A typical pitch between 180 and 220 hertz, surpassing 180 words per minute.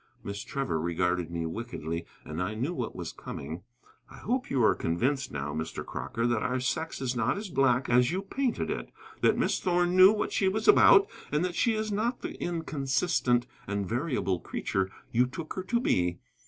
No: low, 125 Hz; average, 195 wpm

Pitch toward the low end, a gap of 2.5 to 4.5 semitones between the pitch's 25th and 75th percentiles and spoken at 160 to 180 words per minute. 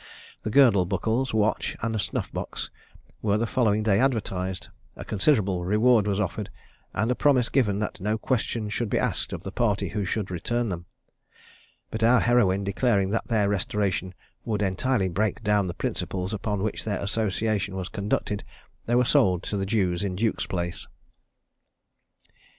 Yes: low, 105 Hz; average, 2.8 semitones; average, 165 wpm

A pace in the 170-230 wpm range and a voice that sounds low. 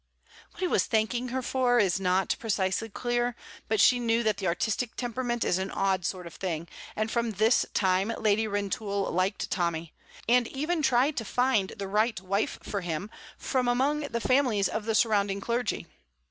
No: average, 175 wpm; high, 220 Hz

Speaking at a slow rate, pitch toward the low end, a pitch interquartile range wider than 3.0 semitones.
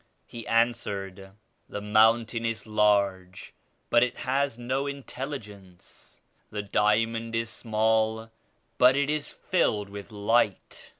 No: slow, 115 wpm; low, 110 Hz; narrow, 2.6 semitones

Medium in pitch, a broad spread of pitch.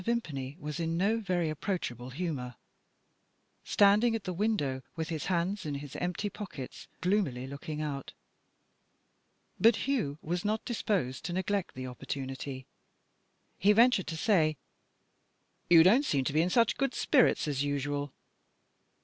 Yes: medium, 170 Hz; wide, 6.4 semitones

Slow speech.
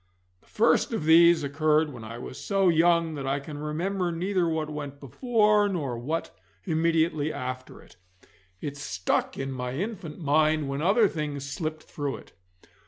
No: average, 165 wpm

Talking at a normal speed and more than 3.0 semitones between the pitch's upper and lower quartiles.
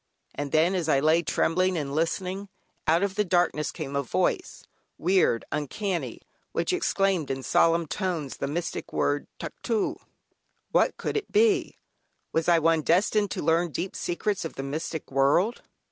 Yes: average, 155 wpm; average, 4.0 semitones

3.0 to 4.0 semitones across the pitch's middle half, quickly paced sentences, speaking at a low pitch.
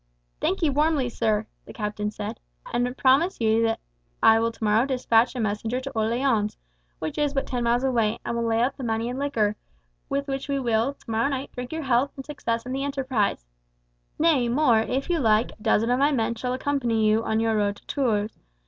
No: average, 3.5 semitones; fast, 210 wpm; high, 240 Hz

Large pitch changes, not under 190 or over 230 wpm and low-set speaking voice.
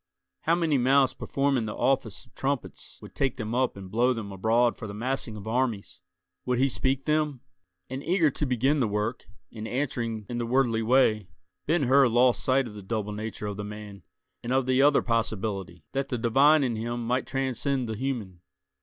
No: average, 3.7 semitones; average, 200 wpm; low, 120 Hz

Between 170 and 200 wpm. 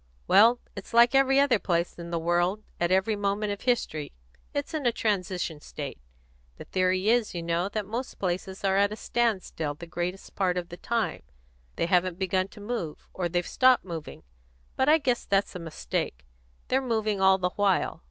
Yes: average, 190 wpm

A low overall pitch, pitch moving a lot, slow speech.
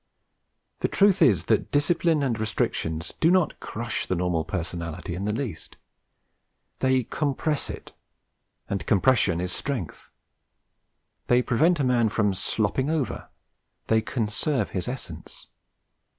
Yes: low, 115 Hz; wide, 7.1 semitones; slow, 125 wpm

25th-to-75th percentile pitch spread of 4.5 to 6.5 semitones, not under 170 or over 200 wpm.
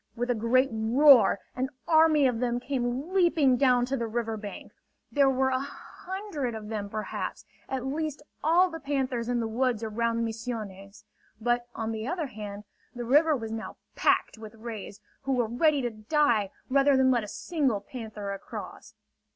No: average, 3.8 semitones; average, 175 wpm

